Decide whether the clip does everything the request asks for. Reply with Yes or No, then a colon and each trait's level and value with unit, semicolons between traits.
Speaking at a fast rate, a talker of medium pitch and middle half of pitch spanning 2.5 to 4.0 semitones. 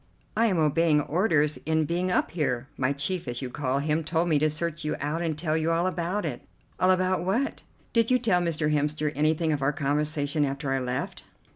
Yes: fast, 215 wpm; medium, 155 Hz; average, 2.9 semitones